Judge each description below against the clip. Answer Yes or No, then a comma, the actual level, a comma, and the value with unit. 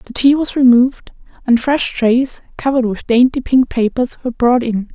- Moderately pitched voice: No, high, 245 Hz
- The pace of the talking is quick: No, average, 180 wpm